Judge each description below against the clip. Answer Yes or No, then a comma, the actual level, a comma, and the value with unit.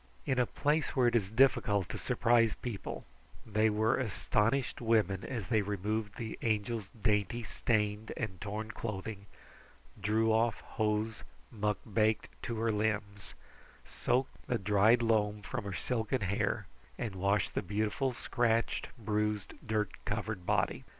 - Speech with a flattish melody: Yes, narrow, 2.0 semitones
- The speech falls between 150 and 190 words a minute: No, average, 140 wpm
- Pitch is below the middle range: Yes, low, 110 Hz